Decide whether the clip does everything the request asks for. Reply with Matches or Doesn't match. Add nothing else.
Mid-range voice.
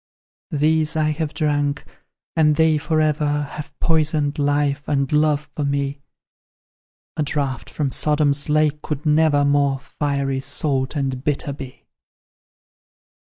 Matches